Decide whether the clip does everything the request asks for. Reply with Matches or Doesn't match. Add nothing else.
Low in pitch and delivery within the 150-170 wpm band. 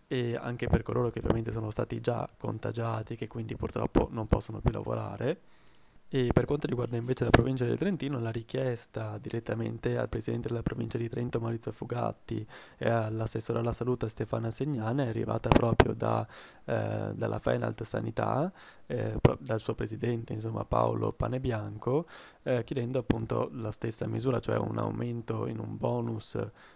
Matches